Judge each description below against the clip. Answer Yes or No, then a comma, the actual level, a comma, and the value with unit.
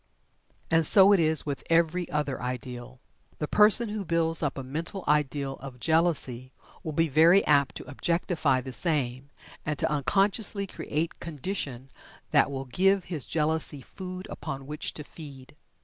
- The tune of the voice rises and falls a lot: No, average, 4.0 semitones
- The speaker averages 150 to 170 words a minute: Yes, average, 155 wpm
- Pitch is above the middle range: No, medium, 150 Hz